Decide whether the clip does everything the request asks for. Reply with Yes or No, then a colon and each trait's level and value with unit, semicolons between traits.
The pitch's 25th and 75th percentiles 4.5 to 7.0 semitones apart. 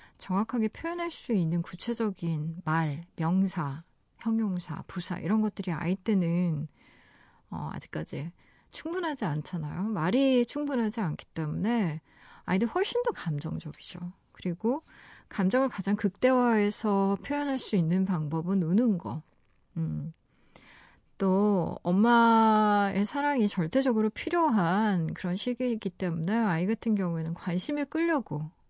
Yes: average, 5.1 semitones